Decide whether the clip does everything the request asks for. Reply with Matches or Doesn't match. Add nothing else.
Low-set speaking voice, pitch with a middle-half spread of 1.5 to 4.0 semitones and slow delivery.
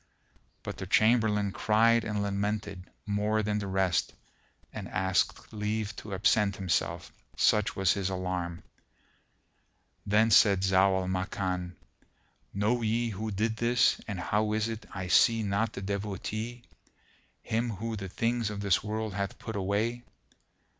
Doesn't match